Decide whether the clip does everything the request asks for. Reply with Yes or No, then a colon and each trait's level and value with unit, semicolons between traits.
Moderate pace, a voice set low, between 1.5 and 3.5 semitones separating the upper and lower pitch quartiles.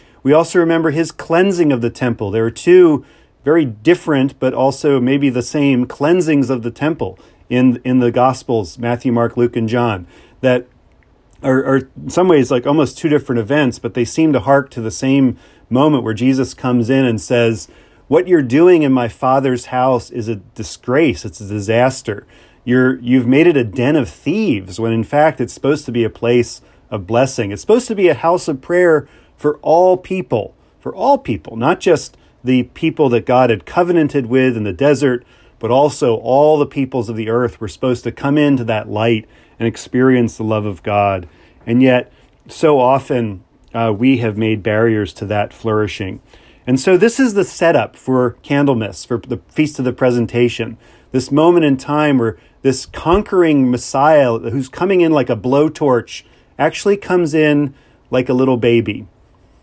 No: average, 185 wpm; low, 125 Hz; average, 4.0 semitones